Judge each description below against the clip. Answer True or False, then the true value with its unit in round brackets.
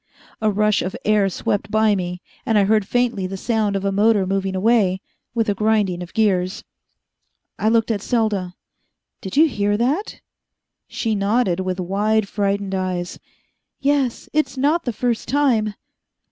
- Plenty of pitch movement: False (2.9 semitones)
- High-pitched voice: True (210 Hz)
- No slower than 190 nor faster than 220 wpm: False (160 wpm)